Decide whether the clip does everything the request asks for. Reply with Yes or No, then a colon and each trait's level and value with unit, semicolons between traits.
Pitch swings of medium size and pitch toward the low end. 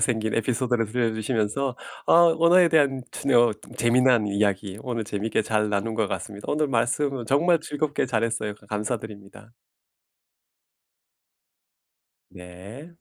Yes: average, 4.1 semitones; low, 115 Hz